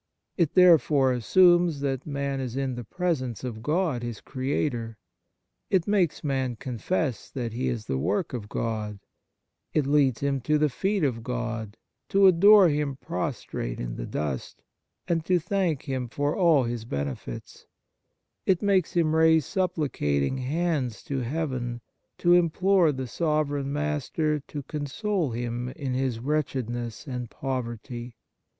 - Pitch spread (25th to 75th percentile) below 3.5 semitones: No, average, 5.1 semitones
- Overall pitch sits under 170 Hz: Yes, medium, 140 Hz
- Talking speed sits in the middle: Yes, average, 145 wpm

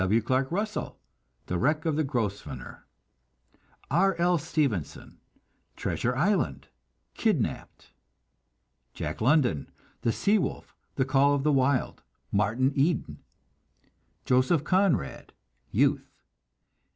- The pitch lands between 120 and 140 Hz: Yes, low, 135 Hz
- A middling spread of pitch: No, wide, 6.0 semitones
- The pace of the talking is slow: Yes, slow, 105 wpm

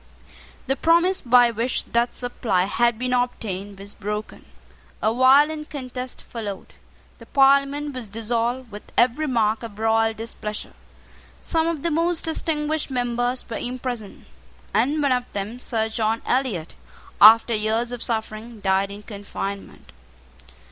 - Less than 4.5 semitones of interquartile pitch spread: Yes, average, 3.3 semitones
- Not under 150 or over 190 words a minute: No, slow, 135 wpm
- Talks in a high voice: Yes, high, 240 Hz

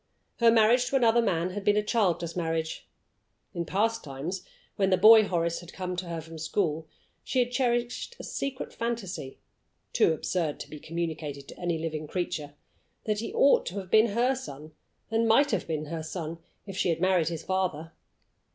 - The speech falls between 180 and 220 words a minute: Yes, average, 190 wpm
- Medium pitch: Yes, medium, 180 Hz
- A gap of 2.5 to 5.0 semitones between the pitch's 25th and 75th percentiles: No, wide, 5.5 semitones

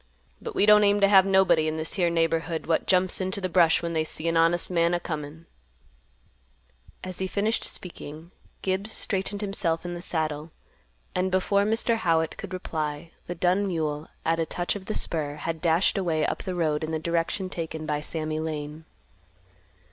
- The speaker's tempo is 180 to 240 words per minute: Yes, average, 185 wpm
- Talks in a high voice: No, medium, 170 Hz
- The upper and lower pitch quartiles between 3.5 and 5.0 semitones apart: No, average, 2.9 semitones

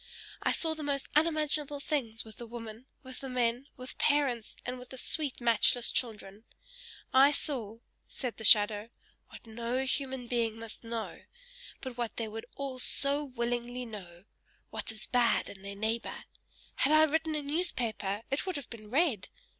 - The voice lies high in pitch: Yes, high, 245 Hz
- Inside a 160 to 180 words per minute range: Yes, average, 170 wpm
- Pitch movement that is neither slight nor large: Yes, average, 3.8 semitones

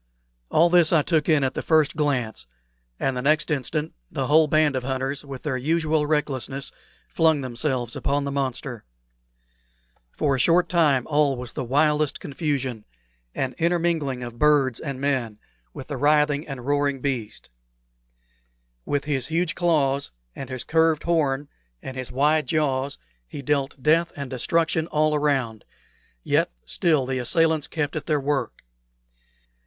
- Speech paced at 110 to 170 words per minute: Yes, average, 150 wpm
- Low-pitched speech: No, medium, 145 Hz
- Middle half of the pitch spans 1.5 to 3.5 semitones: Yes, average, 2.7 semitones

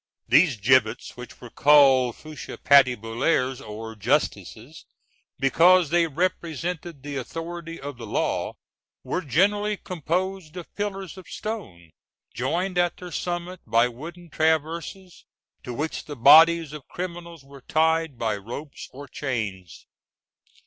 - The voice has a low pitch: No, medium, 155 Hz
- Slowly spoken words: Yes, slow, 125 wpm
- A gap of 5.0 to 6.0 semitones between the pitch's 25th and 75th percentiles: Yes, wide, 5.4 semitones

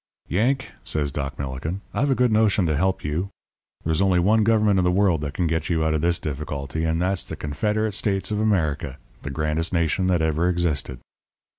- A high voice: No, very low, 85 Hz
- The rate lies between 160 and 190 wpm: No, average, 200 wpm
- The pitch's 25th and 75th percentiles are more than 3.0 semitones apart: Yes, average, 4.4 semitones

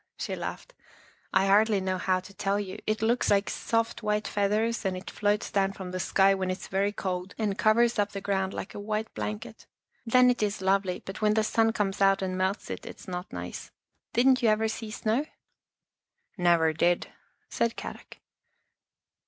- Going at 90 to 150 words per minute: No, average, 195 wpm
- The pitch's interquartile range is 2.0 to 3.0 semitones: Yes, narrow, 2.5 semitones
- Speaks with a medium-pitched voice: No, high, 205 Hz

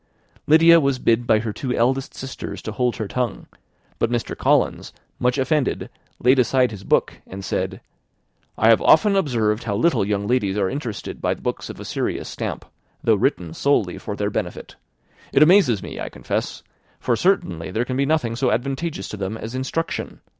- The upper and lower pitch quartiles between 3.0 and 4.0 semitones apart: No, average, 4.4 semitones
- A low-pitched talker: Yes, low, 120 Hz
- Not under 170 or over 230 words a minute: Yes, average, 180 wpm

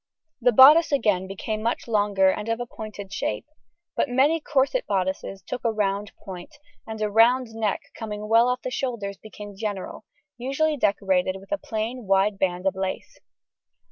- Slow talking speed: No, average, 175 wpm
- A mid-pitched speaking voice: No, high, 215 Hz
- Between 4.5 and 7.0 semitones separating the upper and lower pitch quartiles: No, average, 4.0 semitones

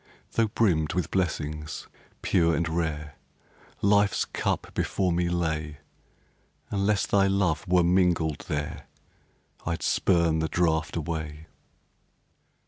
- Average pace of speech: No, slow, 110 wpm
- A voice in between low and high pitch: No, very low, 85 Hz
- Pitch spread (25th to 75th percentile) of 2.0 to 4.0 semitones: Yes, average, 2.9 semitones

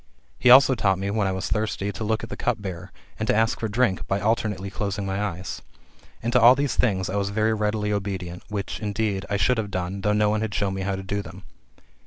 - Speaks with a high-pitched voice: No, low, 105 Hz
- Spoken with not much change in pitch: Yes, narrow, 2.2 semitones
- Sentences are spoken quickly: Yes, fast, 250 wpm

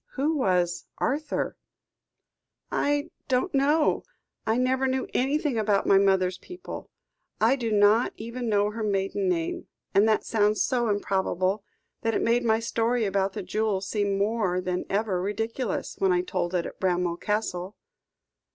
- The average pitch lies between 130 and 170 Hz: No, high, 210 Hz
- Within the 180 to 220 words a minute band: No, average, 150 wpm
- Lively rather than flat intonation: No, average, 4.0 semitones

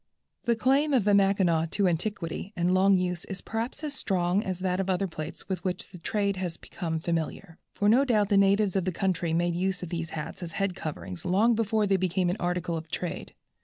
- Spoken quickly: Yes, fast, 225 wpm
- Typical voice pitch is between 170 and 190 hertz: Yes, medium, 185 Hz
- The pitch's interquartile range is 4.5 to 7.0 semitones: No, narrow, 2.6 semitones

